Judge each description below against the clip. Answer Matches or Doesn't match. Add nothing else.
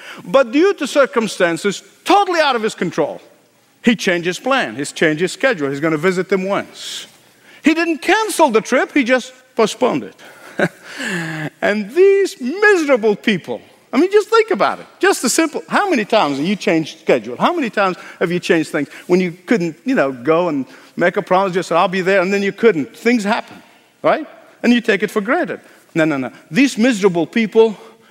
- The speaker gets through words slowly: Doesn't match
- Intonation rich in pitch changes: Matches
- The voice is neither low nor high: Doesn't match